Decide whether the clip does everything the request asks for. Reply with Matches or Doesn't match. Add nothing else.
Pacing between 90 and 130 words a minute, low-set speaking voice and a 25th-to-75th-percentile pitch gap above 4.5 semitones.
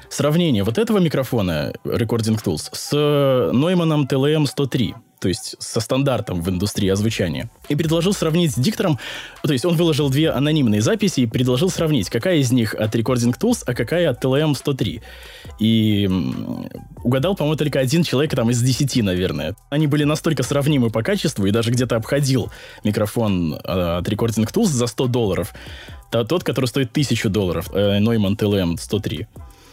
Doesn't match